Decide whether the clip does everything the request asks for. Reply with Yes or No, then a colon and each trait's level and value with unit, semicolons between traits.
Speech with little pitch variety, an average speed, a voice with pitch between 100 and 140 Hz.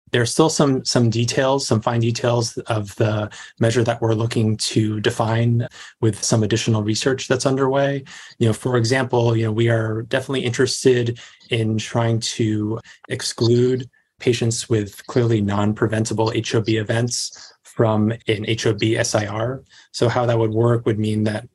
Yes: narrow, 1.8 semitones; average, 155 wpm; low, 115 Hz